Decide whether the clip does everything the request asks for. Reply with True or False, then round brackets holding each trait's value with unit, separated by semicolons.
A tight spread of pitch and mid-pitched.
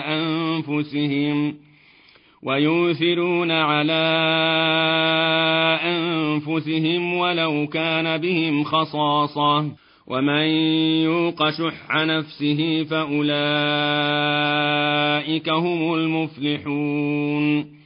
True (1.5 semitones; 155 Hz)